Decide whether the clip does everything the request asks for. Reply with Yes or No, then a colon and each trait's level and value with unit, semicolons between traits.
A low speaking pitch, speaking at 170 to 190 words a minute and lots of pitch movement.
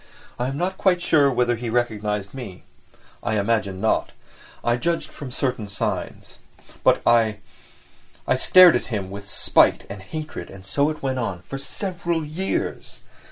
No: low, 120 Hz; average, 155 wpm; wide, 6.5 semitones